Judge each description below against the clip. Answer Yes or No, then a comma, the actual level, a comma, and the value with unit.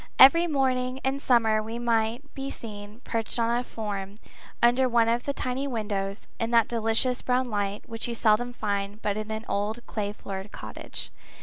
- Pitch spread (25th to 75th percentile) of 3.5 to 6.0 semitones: No, average, 2.8 semitones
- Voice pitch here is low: No, high, 230 Hz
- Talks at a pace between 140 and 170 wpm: No, average, 180 wpm